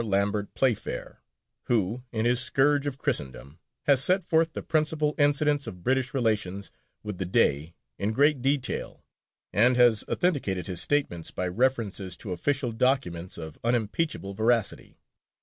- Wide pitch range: Yes, wide, 6.3 semitones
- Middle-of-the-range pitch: No, low, 120 Hz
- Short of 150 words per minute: Yes, average, 140 wpm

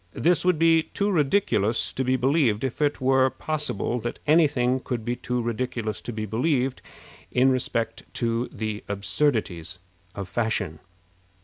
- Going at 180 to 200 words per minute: No, average, 150 wpm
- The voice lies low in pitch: Yes, low, 125 Hz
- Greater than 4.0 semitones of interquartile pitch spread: Yes, average, 4.6 semitones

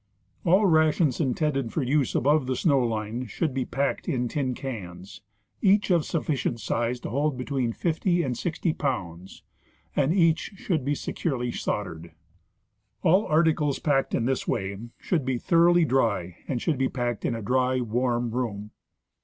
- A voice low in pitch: Yes, low, 130 Hz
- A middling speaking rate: Yes, average, 160 wpm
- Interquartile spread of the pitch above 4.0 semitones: Yes, average, 4.7 semitones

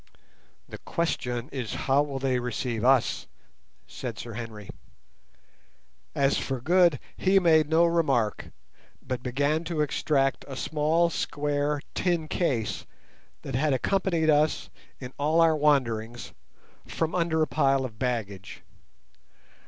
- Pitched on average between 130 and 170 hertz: Yes, medium, 140 Hz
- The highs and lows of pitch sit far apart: No, average, 4.3 semitones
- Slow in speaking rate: Yes, slow, 125 wpm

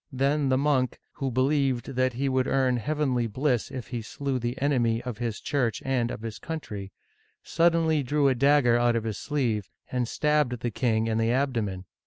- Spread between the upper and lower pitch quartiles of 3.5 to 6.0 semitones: No, average, 3.1 semitones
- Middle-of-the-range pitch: No, low, 130 Hz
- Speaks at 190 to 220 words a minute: Yes, average, 200 wpm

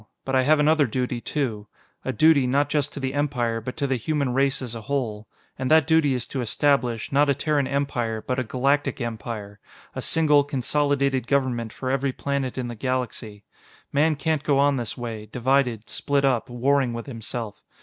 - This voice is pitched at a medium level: No, low, 130 Hz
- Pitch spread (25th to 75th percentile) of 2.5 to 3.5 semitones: Yes, average, 3.1 semitones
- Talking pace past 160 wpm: Yes, average, 190 wpm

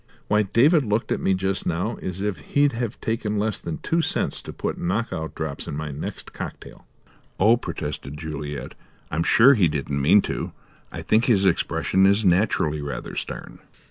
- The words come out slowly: No, average, 180 wpm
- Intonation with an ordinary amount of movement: No, wide, 6.1 semitones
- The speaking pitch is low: Yes, very low, 95 Hz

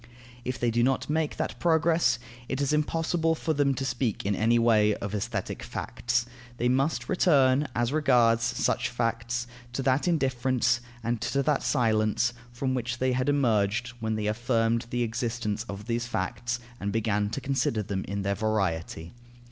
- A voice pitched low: Yes, low, 120 Hz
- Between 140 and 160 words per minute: No, average, 170 wpm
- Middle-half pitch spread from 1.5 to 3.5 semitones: Yes, average, 3.2 semitones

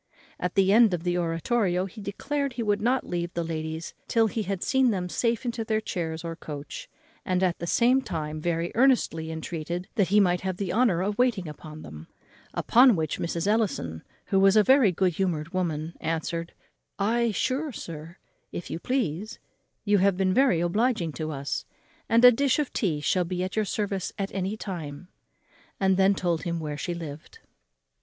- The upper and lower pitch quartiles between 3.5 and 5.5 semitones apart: Yes, average, 4.8 semitones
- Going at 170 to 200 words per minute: Yes, average, 190 wpm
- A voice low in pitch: No, medium, 185 Hz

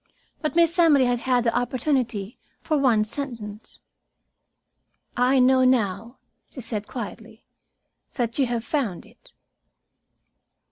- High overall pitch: Yes, high, 245 Hz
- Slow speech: Yes, slow, 120 wpm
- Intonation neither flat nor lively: Yes, average, 3.0 semitones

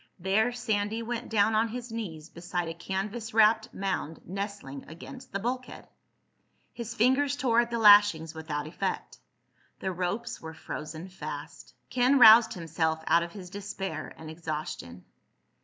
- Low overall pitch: No, high, 195 Hz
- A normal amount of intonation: No, wide, 5.8 semitones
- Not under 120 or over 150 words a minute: Yes, average, 145 wpm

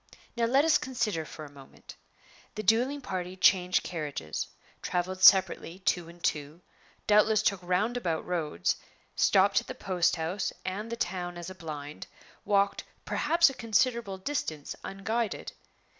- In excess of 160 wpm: No, average, 145 wpm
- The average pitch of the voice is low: No, medium, 185 Hz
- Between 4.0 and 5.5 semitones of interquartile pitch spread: Yes, average, 4.4 semitones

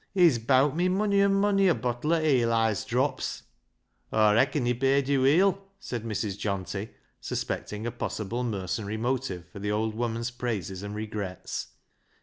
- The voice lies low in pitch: Yes, low, 120 Hz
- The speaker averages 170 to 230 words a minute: No, average, 160 wpm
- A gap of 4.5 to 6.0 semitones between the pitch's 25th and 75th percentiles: Yes, average, 4.9 semitones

